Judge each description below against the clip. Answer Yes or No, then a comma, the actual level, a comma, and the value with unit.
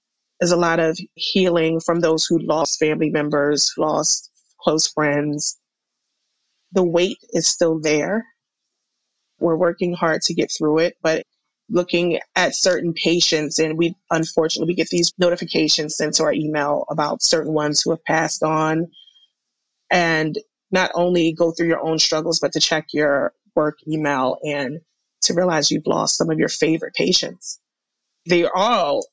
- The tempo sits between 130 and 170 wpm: Yes, average, 155 wpm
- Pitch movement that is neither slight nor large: No, narrow, 2.0 semitones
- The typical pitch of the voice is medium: Yes, medium, 160 Hz